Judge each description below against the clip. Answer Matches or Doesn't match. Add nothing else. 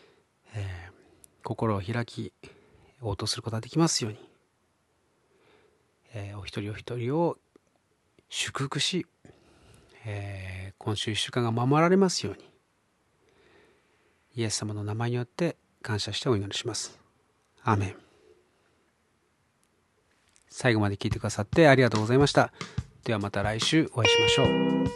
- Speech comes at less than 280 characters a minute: Matches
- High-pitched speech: Doesn't match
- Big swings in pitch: Doesn't match